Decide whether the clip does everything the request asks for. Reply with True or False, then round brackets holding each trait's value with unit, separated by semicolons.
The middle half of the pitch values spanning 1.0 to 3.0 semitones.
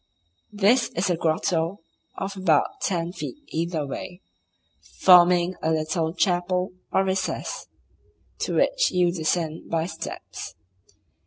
True (2.4 semitones)